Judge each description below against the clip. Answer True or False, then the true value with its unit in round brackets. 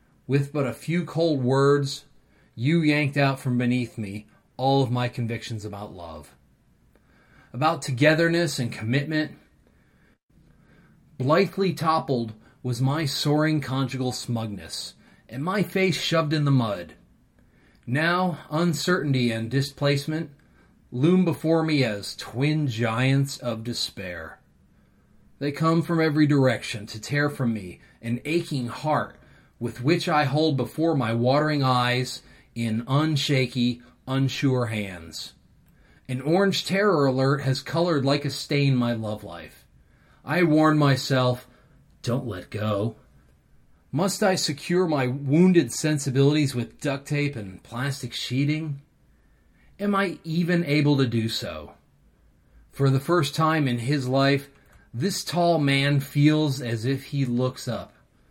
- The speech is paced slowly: True (130 wpm)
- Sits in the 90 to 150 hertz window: True (140 Hz)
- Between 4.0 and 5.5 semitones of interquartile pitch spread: True (4.3 semitones)